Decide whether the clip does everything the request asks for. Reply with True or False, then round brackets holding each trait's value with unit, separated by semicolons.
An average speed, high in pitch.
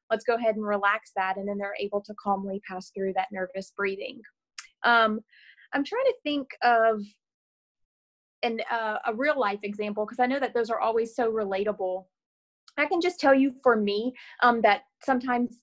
True (185 wpm; 225 Hz)